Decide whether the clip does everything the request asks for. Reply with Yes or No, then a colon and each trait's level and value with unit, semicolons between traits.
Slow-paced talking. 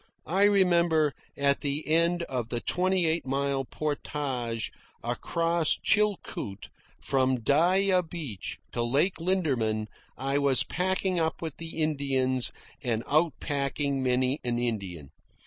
Yes: slow, 125 wpm